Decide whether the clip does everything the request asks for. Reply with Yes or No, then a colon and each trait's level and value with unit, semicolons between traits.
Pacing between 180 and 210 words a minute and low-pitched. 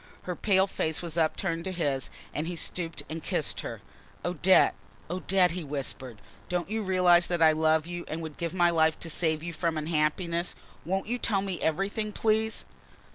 No: average, 185 wpm; medium, 170 Hz